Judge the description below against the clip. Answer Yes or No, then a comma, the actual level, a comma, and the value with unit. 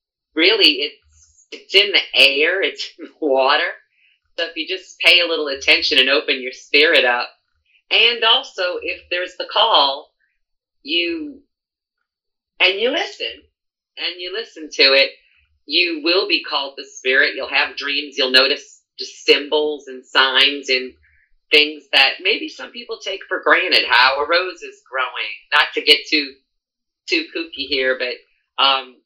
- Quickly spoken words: No, average, 155 wpm